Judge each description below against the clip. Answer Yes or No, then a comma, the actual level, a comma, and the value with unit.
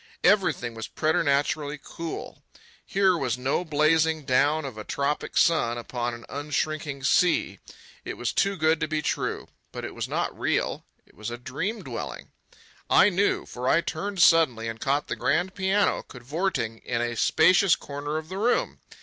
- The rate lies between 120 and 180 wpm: Yes, average, 165 wpm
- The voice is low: No, medium, 150 Hz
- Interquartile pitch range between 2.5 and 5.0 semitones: No, wide, 5.4 semitones